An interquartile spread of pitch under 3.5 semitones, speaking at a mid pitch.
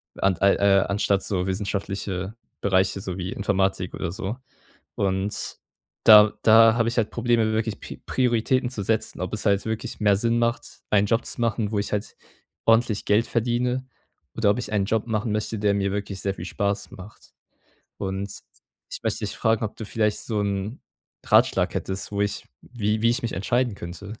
No: narrow, 2.4 semitones; low, 105 Hz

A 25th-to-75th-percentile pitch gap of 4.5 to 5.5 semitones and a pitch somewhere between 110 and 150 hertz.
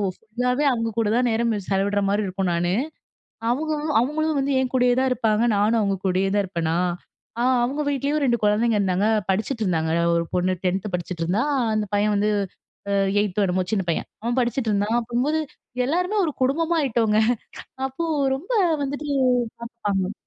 No: average, 4.9 semitones; high, 220 Hz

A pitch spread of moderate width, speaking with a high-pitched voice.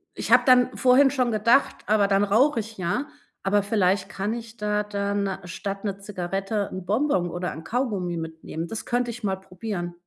Yes: average, 3.5 semitones; high, 205 Hz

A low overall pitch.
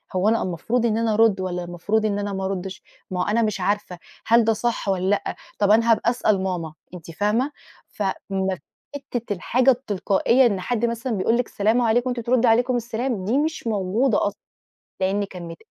No: high, 215 Hz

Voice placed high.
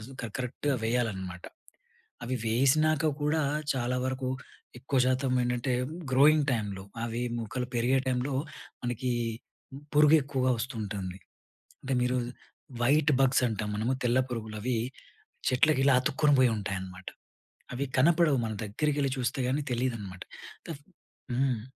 No: low, 125 Hz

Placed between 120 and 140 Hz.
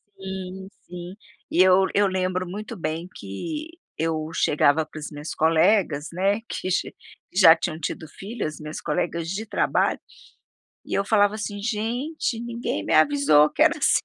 No: medium, 185 Hz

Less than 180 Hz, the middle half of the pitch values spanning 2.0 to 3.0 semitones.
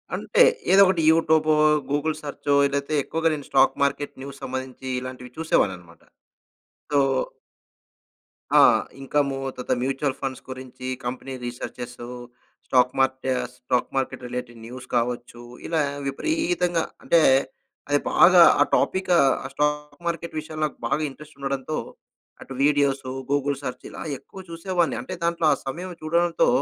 No: medium, 140 Hz; average, 3.7 semitones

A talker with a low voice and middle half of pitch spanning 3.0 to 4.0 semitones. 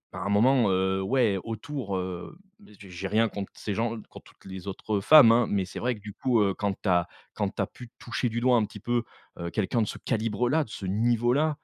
Yes: low, 110 Hz; average, 3.7 semitones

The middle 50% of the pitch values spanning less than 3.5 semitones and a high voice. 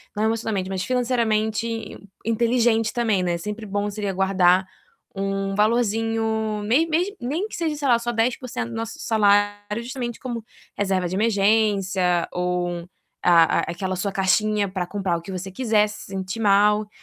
Yes: average, 3.0 semitones; high, 210 Hz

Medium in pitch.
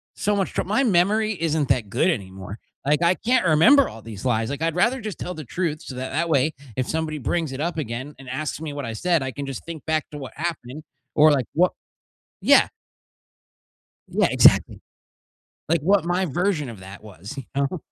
Yes: medium, 155 Hz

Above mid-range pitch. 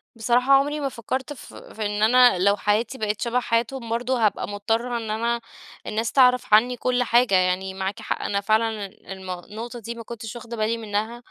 Yes: high, 230 Hz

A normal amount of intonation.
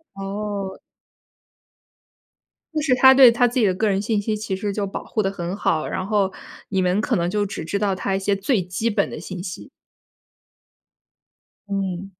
No: narrow, 1.9 semitones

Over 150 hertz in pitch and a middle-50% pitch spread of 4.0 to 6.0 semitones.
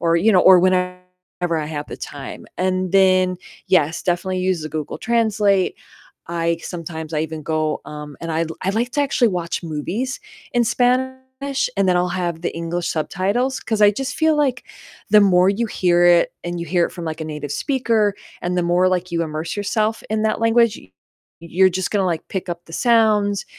Yes: medium, 185 Hz; average, 4.4 semitones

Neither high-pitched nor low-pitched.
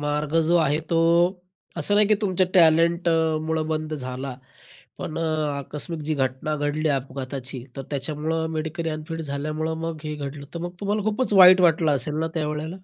Yes: medium, 155 Hz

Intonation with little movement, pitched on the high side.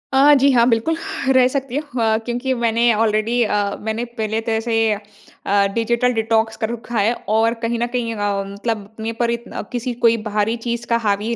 Yes: narrow, 1.6 semitones; high, 230 Hz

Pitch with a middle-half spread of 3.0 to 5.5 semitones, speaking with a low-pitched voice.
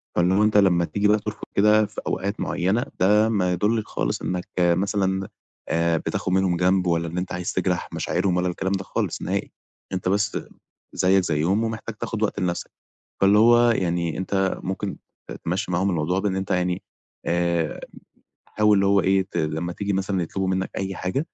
No: narrow, 2.4 semitones; very low, 95 Hz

